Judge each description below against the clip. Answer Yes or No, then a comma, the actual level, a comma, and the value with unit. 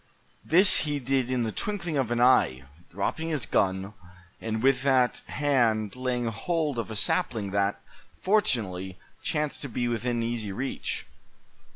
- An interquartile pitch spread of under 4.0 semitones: No, average, 4.3 semitones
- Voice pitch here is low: Yes, low, 120 Hz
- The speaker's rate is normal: Yes, average, 150 wpm